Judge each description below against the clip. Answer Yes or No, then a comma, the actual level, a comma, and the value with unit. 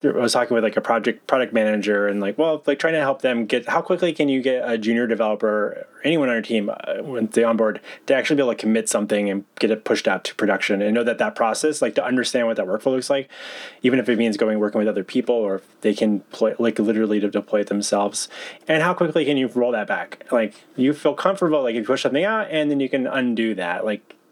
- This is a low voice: Yes, low, 115 Hz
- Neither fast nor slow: No, fast, 265 wpm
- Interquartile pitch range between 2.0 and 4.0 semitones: No, average, 4.7 semitones